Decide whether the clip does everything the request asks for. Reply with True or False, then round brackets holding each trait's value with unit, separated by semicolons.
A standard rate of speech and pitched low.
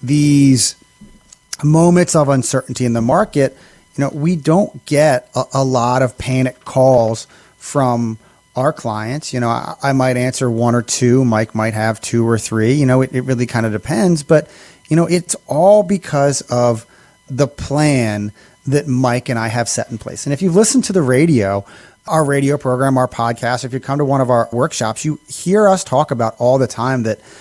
True (195 wpm; 130 Hz)